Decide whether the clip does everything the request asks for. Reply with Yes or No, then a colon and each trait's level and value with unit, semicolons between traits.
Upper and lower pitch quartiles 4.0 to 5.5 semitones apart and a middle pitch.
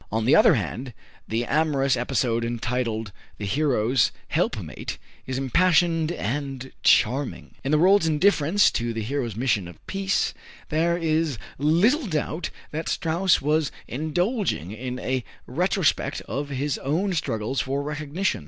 Yes: average, 4.8 semitones; medium, 145 Hz